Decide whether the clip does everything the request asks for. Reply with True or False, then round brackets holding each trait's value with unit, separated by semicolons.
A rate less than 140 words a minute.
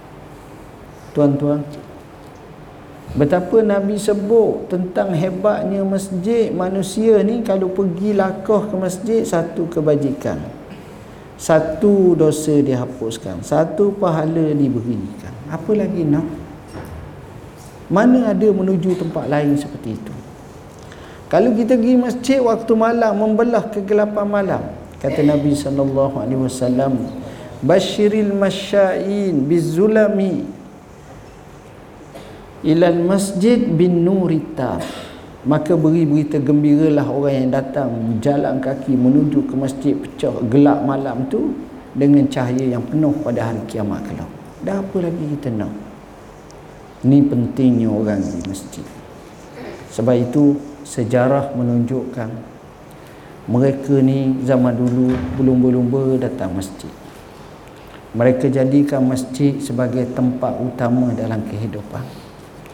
True (100 wpm)